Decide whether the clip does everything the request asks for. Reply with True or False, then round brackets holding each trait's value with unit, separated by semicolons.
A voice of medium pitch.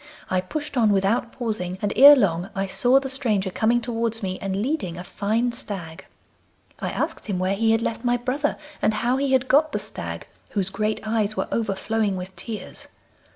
False (220 Hz)